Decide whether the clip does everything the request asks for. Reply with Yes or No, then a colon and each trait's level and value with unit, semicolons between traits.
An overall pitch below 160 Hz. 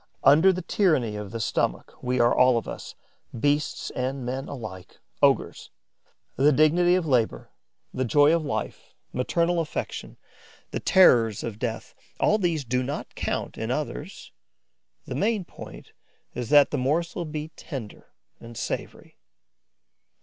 Yes: medium, 140 Hz